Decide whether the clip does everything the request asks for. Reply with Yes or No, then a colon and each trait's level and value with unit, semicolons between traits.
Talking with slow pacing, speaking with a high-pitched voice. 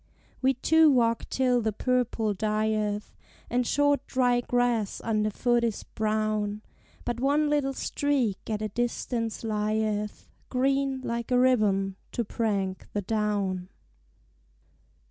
Yes: slow, 125 wpm; high, 230 Hz